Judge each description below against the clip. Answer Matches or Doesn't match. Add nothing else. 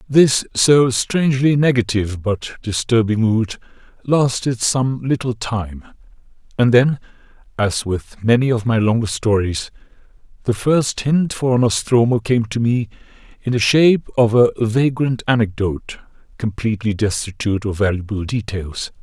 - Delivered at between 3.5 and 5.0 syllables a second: Matches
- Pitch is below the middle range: Matches